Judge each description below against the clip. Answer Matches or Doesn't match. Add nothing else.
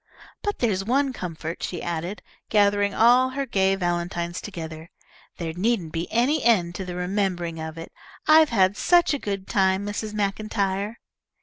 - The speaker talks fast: Doesn't match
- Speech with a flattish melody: Doesn't match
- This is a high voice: Matches